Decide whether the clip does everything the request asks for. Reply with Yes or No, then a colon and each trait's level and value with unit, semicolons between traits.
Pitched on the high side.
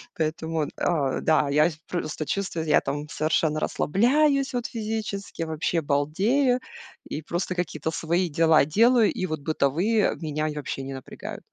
No: medium, 160 Hz